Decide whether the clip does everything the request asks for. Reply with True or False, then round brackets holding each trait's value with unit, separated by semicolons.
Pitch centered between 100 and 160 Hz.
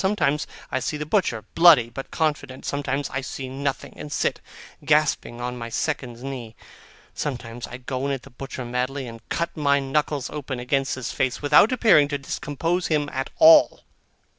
True (135 Hz)